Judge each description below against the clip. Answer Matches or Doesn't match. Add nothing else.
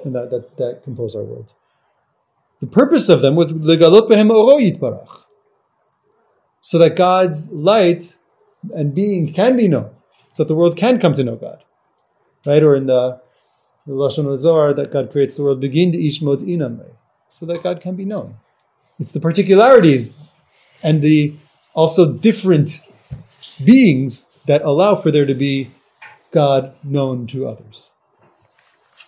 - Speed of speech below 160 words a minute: Matches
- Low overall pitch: Doesn't match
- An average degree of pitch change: Matches